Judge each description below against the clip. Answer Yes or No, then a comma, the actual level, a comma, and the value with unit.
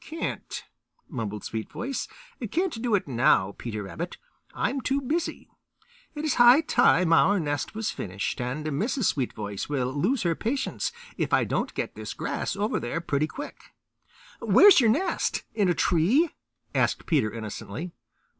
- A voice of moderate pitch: Yes, medium, 175 Hz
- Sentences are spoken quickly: No, average, 155 wpm